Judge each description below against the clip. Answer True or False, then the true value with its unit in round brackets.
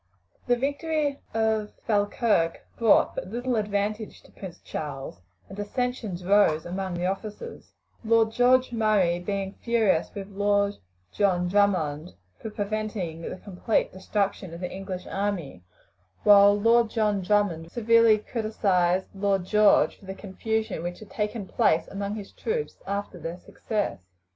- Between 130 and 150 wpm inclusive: True (140 wpm)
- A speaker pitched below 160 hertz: False (205 Hz)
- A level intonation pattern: False (3.0 semitones)